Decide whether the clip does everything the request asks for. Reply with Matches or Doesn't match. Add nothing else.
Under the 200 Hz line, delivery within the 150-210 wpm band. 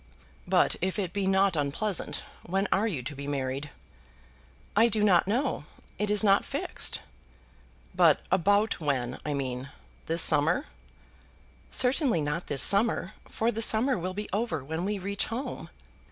Matches